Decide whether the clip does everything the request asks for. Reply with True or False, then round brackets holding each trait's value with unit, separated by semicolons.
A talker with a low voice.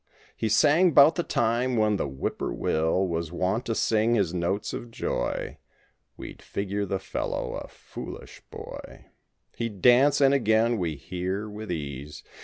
True (105 Hz)